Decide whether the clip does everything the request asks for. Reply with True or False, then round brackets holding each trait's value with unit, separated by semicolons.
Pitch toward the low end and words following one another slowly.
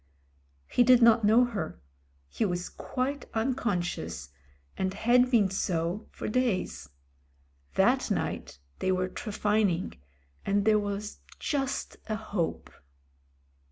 False (210 Hz; 120 wpm)